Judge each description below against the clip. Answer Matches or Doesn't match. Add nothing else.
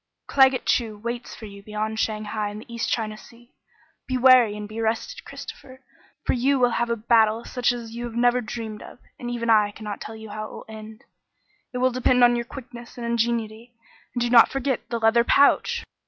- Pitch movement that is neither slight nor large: Doesn't match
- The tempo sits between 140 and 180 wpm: Doesn't match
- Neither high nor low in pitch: Doesn't match